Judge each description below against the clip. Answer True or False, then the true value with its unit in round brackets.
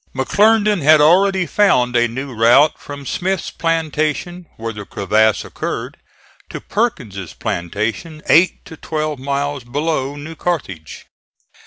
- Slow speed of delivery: True (125 wpm)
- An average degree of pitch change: False (5.8 semitones)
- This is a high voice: False (145 Hz)